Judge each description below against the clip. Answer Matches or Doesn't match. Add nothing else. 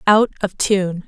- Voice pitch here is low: Doesn't match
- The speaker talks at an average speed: Matches